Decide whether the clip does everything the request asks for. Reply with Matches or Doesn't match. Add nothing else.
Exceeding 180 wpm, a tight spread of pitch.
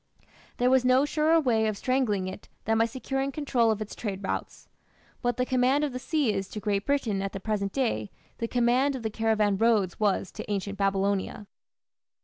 Doesn't match